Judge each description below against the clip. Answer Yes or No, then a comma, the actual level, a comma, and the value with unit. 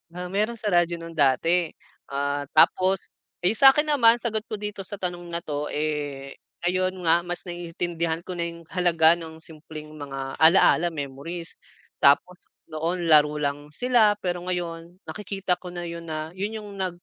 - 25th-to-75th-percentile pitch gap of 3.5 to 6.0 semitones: No, average, 3.1 semitones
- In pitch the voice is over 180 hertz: No, medium, 170 Hz